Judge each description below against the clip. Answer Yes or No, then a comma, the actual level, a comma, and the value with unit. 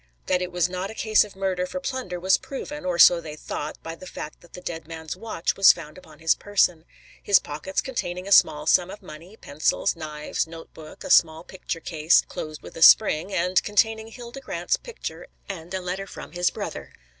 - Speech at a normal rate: No, fast, 210 wpm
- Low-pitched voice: No, medium, 180 Hz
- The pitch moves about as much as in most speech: Yes, average, 3.6 semitones